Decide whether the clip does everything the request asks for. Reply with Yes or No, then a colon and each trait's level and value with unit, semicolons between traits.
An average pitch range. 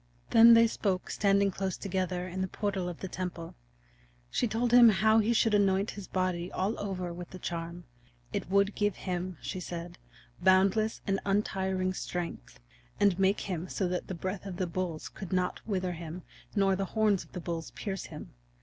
No: narrow, 2.1 semitones